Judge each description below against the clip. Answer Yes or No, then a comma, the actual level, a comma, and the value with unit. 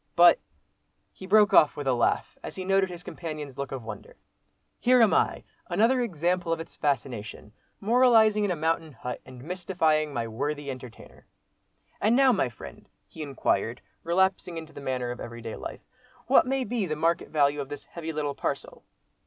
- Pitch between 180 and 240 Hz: No, medium, 160 Hz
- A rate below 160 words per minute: No, average, 180 wpm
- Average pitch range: No, wide, 6.1 semitones